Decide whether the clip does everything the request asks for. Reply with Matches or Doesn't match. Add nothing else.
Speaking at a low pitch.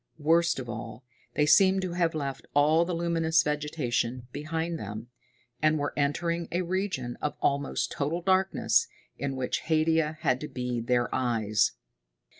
Doesn't match